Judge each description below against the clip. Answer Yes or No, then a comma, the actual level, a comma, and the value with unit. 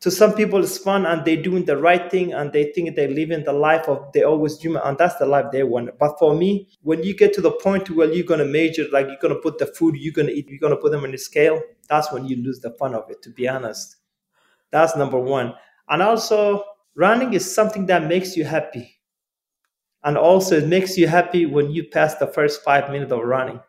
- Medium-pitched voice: Yes, medium, 160 Hz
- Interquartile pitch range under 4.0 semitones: No, average, 4.7 semitones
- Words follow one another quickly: Yes, fast, 245 wpm